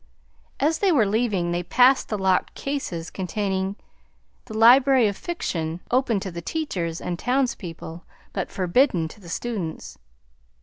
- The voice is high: Yes, high, 200 Hz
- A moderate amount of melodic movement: No, wide, 6.6 semitones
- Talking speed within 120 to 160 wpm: Yes, average, 140 wpm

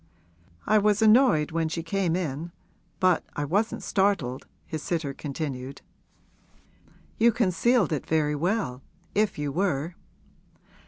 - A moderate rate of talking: No, slow, 120 wpm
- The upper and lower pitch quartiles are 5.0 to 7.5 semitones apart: Yes, wide, 5.5 semitones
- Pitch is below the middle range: No, medium, 170 Hz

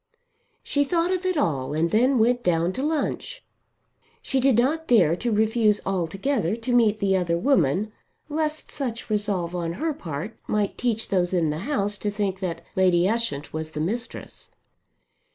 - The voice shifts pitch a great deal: Yes, wide, 6.2 semitones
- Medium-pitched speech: No, high, 210 Hz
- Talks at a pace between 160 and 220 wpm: Yes, average, 170 wpm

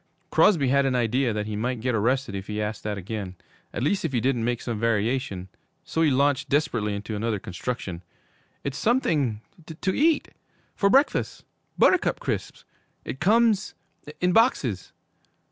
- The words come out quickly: No, average, 160 wpm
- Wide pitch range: Yes, wide, 6.1 semitones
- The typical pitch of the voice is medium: No, low, 125 Hz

